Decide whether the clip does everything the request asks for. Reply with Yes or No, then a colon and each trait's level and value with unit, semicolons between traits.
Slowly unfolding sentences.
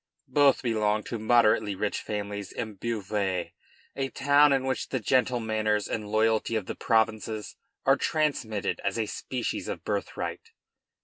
No: average, 145 wpm